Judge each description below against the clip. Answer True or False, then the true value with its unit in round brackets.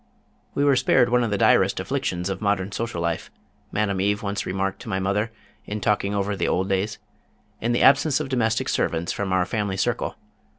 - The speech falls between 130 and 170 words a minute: False (200 wpm)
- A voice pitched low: True (100 Hz)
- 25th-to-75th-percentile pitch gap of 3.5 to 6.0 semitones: False (3.0 semitones)